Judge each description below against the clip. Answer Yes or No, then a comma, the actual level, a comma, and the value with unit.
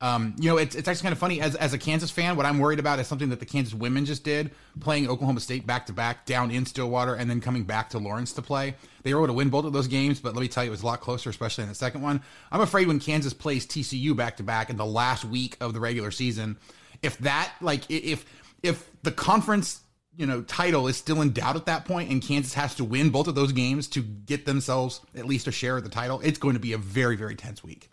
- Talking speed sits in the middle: No, fast, 275 wpm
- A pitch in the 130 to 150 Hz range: Yes, low, 135 Hz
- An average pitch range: Yes, average, 3.5 semitones